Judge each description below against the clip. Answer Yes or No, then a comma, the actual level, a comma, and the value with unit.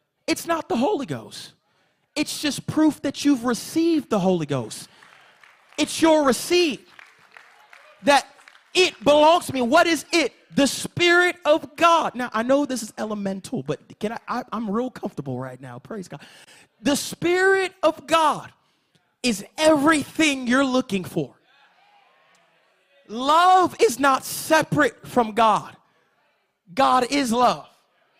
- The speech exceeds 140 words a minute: No, slow, 135 wpm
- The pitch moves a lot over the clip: Yes, wide, 6.3 semitones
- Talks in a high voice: Yes, very high, 275 Hz